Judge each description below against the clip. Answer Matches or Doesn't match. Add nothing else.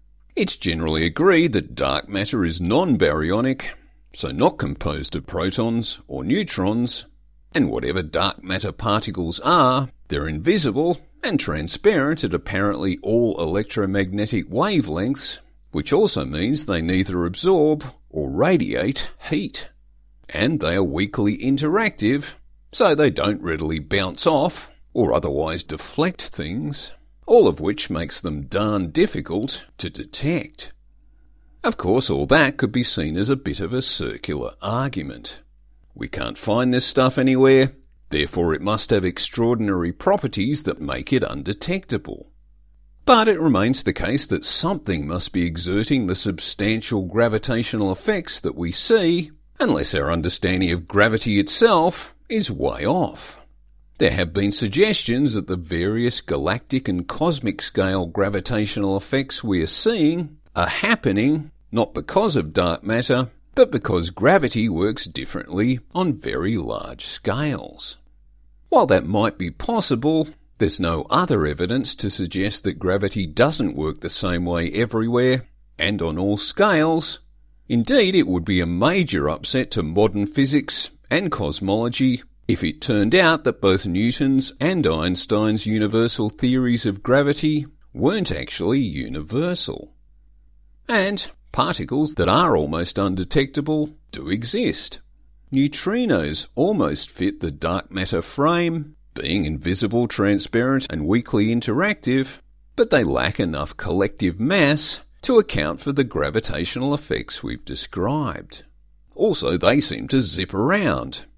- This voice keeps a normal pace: Doesn't match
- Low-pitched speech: Matches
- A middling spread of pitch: Doesn't match